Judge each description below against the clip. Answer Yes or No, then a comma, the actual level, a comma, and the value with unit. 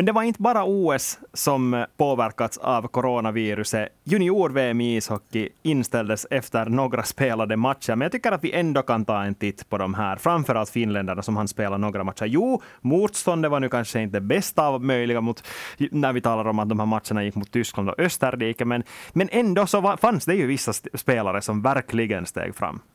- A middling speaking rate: No, fast, 200 wpm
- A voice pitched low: Yes, low, 120 Hz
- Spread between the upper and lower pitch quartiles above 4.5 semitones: Yes, average, 5.2 semitones